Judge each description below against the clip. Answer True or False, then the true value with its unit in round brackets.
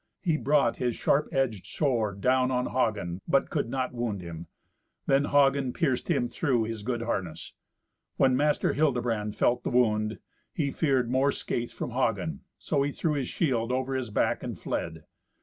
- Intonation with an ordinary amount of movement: True (3.6 semitones)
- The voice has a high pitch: False (125 Hz)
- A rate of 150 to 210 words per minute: True (170 wpm)